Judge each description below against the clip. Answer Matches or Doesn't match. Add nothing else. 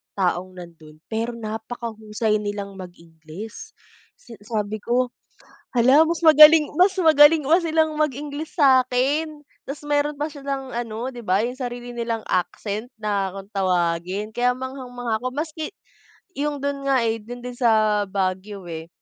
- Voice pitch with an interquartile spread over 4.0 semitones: Matches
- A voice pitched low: Doesn't match